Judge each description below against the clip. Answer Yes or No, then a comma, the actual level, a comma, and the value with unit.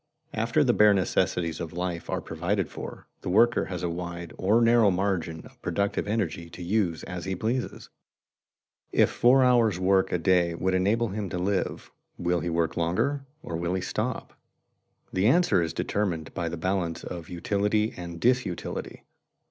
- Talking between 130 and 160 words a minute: No, average, 170 wpm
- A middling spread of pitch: Yes, average, 3.5 semitones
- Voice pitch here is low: Yes, very low, 95 Hz